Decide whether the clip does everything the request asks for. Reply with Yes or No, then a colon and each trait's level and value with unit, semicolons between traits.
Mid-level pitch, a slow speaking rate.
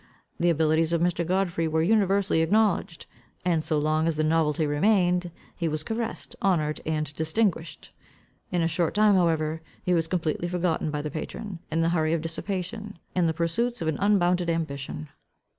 No: medium, 165 Hz; average, 175 wpm